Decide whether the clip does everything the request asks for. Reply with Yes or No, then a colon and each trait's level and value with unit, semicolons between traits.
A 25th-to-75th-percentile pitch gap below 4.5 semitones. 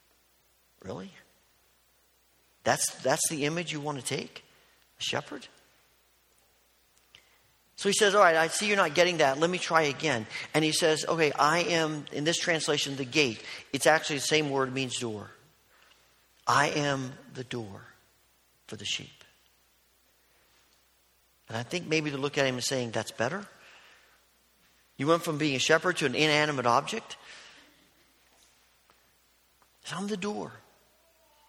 No: wide, 5.5 semitones